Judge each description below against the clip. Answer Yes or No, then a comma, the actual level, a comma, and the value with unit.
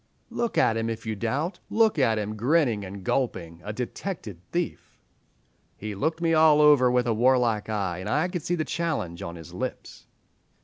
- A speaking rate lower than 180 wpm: No, average, 185 wpm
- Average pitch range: No, wide, 7.1 semitones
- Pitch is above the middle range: No, low, 120 Hz